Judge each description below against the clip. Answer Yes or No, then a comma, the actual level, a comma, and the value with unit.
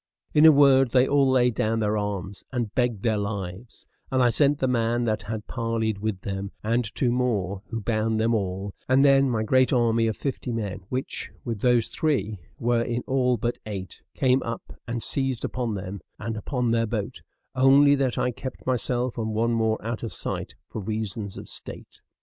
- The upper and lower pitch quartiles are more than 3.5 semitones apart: No, average, 2.9 semitones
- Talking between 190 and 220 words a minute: Yes, average, 195 wpm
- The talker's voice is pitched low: Yes, low, 115 Hz